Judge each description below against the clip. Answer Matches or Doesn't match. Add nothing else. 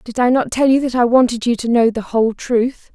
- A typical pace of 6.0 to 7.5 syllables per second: Doesn't match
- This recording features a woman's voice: Matches